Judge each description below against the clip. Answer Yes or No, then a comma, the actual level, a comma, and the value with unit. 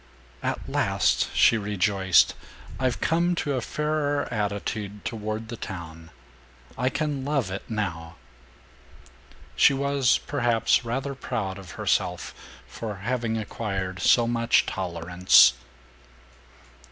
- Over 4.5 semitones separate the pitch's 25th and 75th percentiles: Yes, wide, 5.4 semitones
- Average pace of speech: No, slow, 110 wpm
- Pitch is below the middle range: Yes, low, 110 Hz